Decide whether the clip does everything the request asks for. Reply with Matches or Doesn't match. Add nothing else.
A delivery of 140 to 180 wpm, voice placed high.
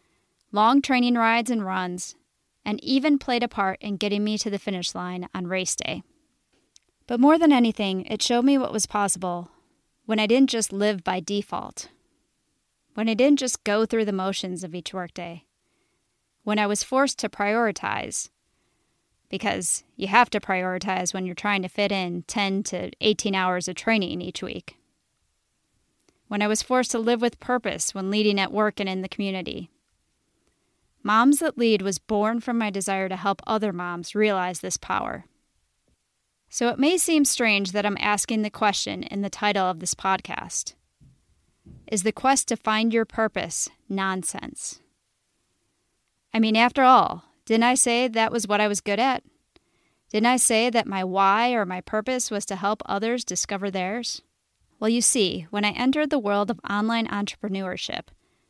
Matches